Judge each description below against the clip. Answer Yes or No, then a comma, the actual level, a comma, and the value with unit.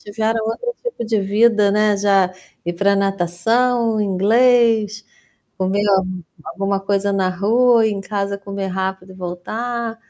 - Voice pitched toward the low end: No, high, 205 Hz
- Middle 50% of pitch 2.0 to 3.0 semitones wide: Yes, narrow, 2.6 semitones